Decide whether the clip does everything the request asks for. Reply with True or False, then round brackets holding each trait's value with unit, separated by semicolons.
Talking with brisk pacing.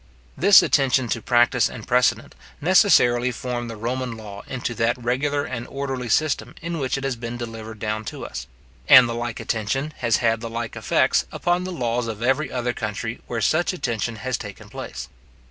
False (185 wpm)